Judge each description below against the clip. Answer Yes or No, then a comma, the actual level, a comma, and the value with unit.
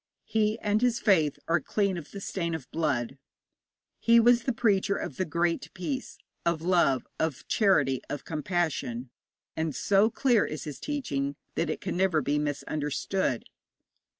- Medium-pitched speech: Yes, medium, 170 Hz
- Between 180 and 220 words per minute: No, average, 155 wpm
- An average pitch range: No, wide, 5.9 semitones